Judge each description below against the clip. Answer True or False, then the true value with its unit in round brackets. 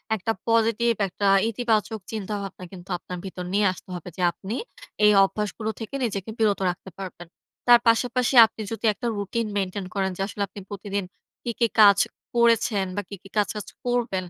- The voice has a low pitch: False (205 Hz)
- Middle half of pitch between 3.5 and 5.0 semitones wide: False (2.8 semitones)